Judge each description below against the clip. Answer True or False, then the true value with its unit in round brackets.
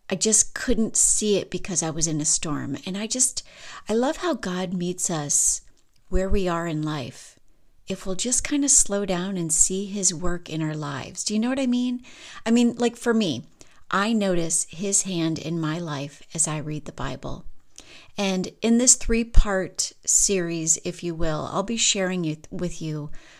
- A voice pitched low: False (185 Hz)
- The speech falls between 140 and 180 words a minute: False (200 wpm)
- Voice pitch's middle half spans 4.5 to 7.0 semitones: True (5.0 semitones)